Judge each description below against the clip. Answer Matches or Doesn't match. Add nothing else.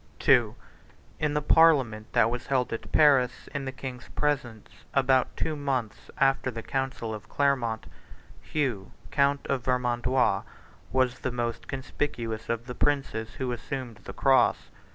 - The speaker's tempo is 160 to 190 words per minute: Doesn't match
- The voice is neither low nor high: Doesn't match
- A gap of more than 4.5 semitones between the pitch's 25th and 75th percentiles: Doesn't match